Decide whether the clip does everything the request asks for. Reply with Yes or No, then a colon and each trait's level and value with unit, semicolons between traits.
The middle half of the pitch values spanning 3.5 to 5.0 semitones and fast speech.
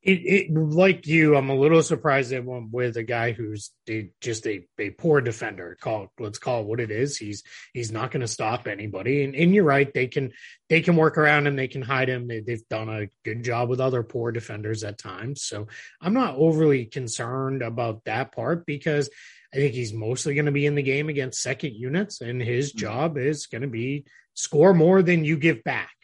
Yes: average, 4.3 semitones; fast, 220 wpm